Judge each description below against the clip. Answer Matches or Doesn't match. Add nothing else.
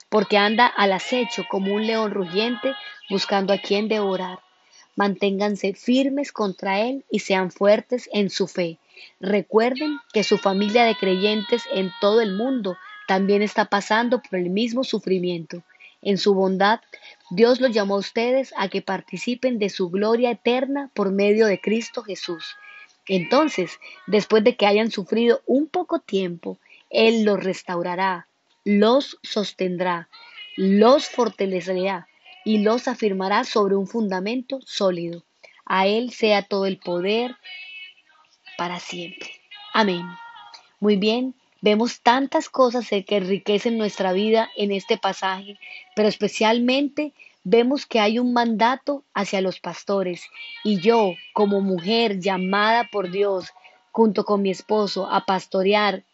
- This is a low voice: Doesn't match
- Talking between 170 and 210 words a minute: Doesn't match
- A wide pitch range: Doesn't match